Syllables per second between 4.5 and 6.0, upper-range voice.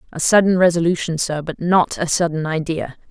No: 5.5 syllables/s; medium, 165 Hz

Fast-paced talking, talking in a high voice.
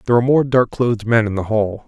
No: fast, 290 wpm; low, 115 Hz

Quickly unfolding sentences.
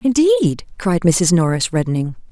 No: slow, 130 wpm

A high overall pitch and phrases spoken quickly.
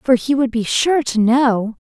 Yes: very high, 250 Hz; fast, 230 wpm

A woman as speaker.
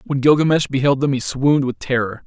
No: male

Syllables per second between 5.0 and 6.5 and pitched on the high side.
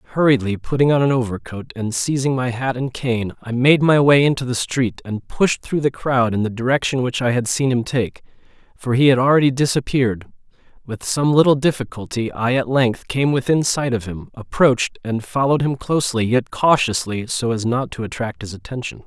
No: 5.3 syllables/s; low, 125 Hz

